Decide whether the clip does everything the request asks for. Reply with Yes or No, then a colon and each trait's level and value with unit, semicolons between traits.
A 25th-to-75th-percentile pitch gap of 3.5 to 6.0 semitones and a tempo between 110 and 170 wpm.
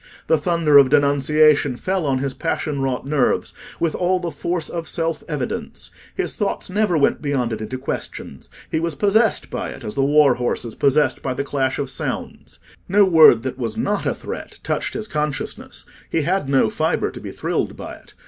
No: average, 3.8 semitones; average, 195 wpm